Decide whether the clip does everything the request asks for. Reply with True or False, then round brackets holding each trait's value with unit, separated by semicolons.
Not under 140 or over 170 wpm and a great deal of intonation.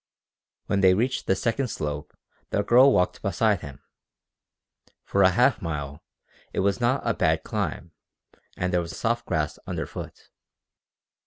True (145 wpm; 6.0 semitones)